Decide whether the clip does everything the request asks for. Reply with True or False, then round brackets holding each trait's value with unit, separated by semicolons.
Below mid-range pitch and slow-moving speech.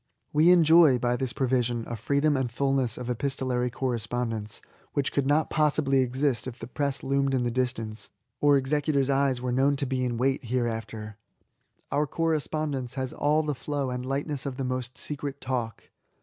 False (130 Hz; 175 wpm)